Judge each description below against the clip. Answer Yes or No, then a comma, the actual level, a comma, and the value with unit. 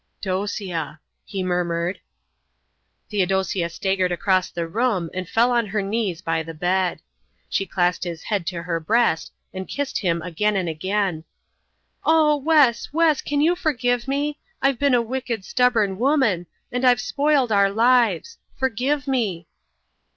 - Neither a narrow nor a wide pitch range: No, wide, 6.0 semitones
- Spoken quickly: No, average, 145 wpm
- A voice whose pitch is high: Yes, high, 205 Hz